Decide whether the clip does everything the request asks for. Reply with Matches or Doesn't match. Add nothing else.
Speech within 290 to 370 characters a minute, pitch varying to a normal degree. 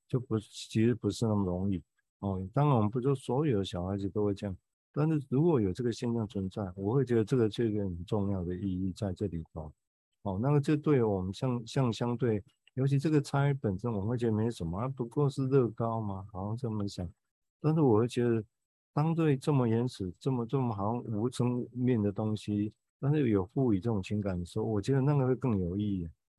Matches